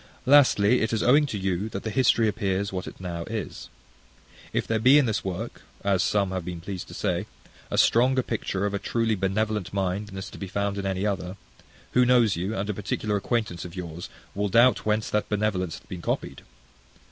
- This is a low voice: Yes, low, 100 Hz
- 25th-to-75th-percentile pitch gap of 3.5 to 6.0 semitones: No, average, 2.7 semitones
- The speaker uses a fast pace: Yes, fast, 215 wpm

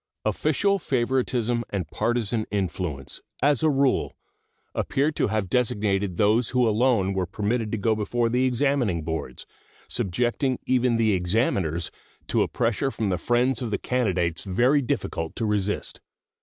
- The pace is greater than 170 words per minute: No, average, 145 wpm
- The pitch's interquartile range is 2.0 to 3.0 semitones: No, average, 4.4 semitones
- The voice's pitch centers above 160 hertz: No, low, 115 Hz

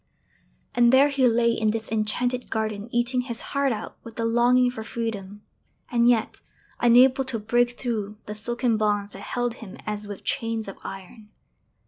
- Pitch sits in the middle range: No, high, 230 Hz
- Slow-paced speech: No, average, 170 wpm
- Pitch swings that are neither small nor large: No, narrow, 2.3 semitones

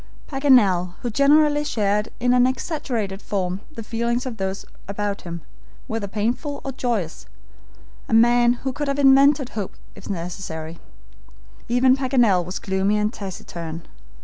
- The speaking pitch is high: Yes, high, 225 Hz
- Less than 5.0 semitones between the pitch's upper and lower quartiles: No, average, 5.3 semitones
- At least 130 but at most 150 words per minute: Yes, average, 140 wpm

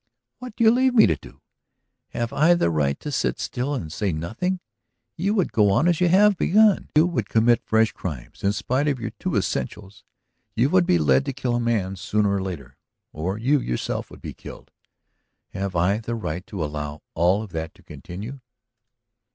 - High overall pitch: No, low, 110 Hz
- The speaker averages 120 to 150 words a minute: No, average, 200 wpm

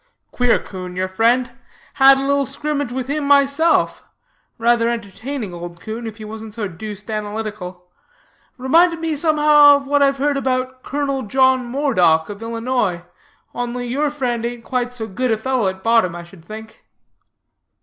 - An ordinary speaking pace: Yes, average, 160 wpm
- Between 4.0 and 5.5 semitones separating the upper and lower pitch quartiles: Yes, average, 4.5 semitones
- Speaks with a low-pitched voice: No, high, 240 Hz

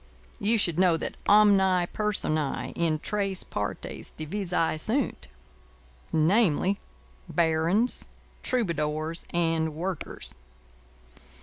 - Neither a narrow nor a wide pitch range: Yes, average, 4.3 semitones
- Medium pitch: Yes, medium, 175 Hz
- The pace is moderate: No, slow, 85 wpm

